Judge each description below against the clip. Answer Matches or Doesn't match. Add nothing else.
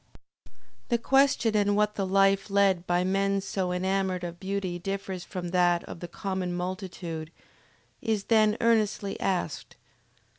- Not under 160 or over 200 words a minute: Doesn't match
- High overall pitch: Matches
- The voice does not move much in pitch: Matches